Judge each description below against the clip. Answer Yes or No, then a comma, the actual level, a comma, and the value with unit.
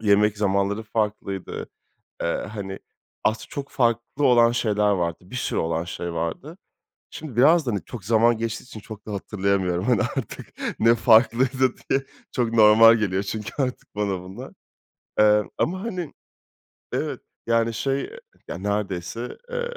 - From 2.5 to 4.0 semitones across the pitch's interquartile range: Yes, average, 3.5 semitones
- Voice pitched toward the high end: No, low, 110 Hz